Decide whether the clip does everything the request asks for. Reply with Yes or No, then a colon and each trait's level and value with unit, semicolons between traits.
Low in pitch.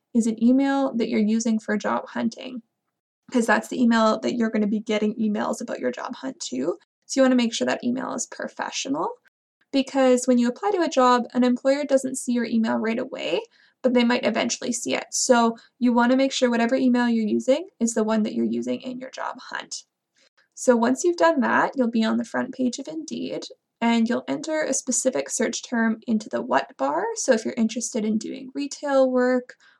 No: high, 245 Hz